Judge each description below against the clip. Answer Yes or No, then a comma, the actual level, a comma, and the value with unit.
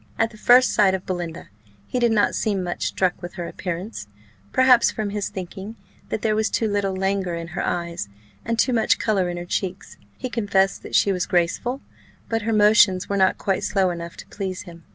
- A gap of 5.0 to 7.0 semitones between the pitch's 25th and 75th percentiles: No, average, 3.5 semitones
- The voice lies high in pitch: Yes, high, 195 Hz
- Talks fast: Yes, fast, 210 wpm